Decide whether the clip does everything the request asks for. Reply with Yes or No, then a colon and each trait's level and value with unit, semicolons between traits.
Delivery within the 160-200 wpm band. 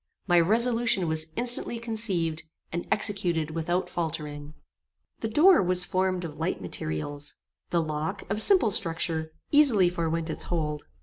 No: slow, 135 wpm